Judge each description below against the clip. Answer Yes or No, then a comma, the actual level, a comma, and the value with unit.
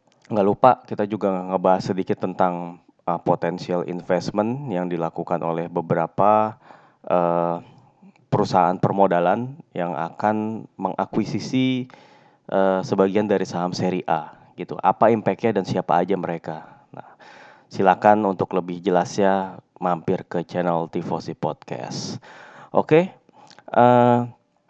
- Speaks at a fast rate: No, average, 110 wpm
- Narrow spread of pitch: No, average, 3.3 semitones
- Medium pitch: No, very low, 95 Hz